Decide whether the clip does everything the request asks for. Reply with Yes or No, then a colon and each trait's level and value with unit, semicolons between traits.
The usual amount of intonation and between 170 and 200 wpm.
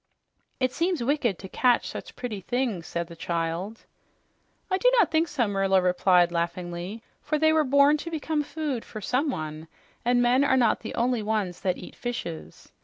No: wide, 7.8 semitones; average, 180 wpm